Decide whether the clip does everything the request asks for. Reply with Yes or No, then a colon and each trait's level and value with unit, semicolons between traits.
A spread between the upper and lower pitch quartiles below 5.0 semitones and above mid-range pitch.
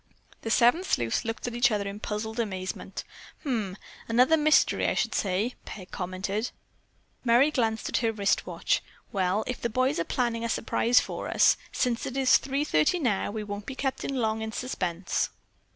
Yes: average, 3.7 semitones; high, 225 Hz